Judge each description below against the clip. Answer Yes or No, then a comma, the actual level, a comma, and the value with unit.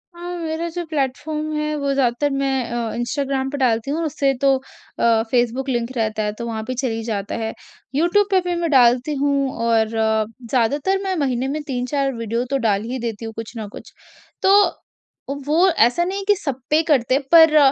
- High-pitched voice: Yes, very high, 270 Hz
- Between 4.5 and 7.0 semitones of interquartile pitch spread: Yes, average, 4.8 semitones